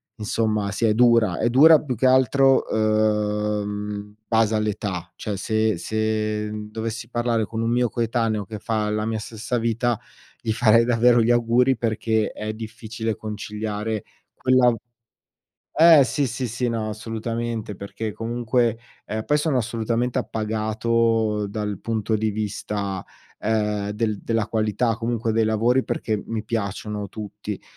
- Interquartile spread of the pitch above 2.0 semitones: No, narrow, 1.7 semitones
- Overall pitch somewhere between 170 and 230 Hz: No, low, 110 Hz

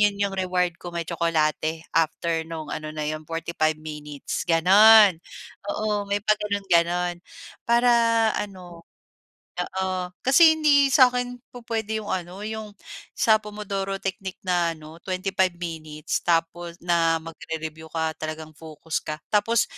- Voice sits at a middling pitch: Yes, medium, 180 Hz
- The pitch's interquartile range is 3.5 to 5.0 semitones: Yes, average, 4.2 semitones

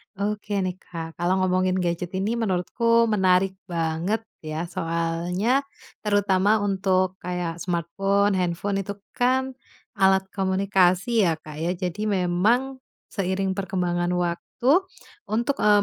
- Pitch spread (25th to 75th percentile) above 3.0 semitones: No, average, 2.7 semitones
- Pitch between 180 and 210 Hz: Yes, high, 190 Hz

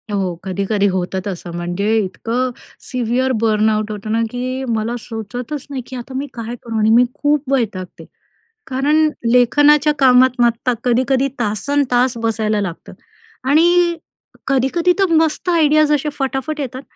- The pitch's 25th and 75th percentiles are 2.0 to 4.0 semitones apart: No, average, 4.6 semitones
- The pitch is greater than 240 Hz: Yes, very high, 250 Hz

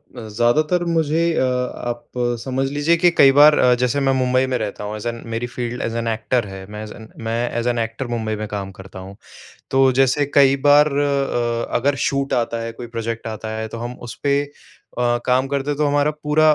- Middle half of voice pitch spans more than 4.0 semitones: No, average, 3.5 semitones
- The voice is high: No, low, 125 Hz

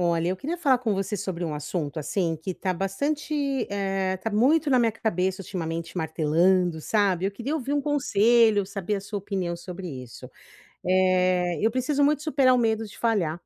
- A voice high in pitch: Yes, high, 195 Hz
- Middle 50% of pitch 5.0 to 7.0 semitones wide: Yes, average, 5.3 semitones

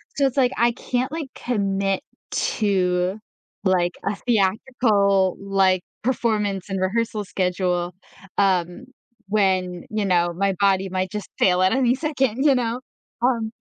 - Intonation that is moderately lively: Yes, average, 4.1 semitones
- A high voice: Yes, high, 200 Hz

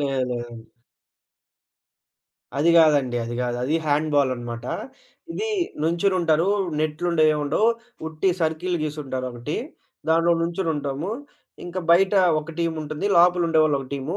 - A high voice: No, medium, 155 Hz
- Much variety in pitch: No, average, 3.8 semitones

